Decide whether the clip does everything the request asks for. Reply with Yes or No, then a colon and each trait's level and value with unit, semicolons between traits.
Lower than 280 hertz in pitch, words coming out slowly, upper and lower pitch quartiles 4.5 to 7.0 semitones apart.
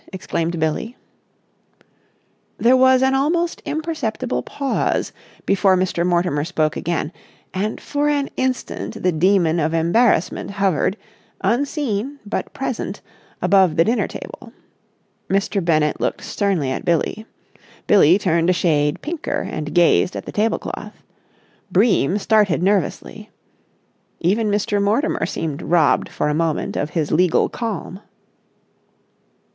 Yes: high, 190 Hz; slow, 120 wpm; wide, 5.6 semitones